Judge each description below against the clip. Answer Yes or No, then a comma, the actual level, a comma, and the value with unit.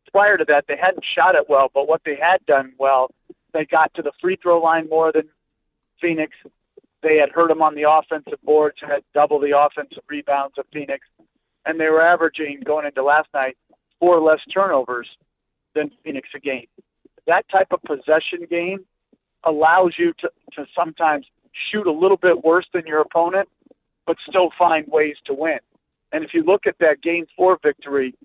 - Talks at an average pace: Yes, average, 185 wpm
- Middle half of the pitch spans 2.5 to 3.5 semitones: Yes, average, 2.9 semitones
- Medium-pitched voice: Yes, medium, 155 Hz